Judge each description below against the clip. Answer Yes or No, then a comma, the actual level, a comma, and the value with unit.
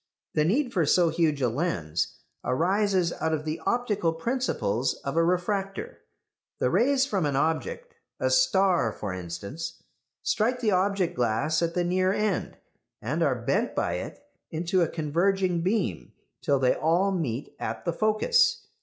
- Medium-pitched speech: Yes, medium, 175 Hz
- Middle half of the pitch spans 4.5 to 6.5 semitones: Yes, average, 5.2 semitones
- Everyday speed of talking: Yes, average, 155 wpm